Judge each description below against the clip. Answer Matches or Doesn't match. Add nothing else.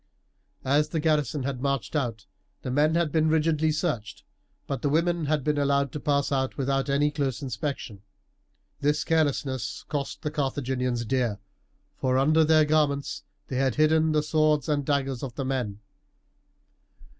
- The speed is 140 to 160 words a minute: Matches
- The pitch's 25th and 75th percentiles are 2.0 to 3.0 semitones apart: Matches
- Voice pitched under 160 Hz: Matches